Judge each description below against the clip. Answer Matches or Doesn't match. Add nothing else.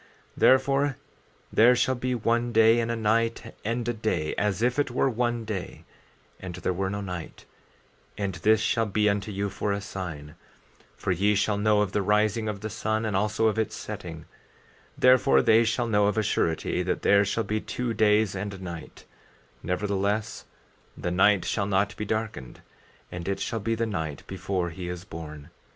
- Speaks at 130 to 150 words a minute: Doesn't match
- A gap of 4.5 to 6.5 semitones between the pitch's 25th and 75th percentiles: Doesn't match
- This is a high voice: Doesn't match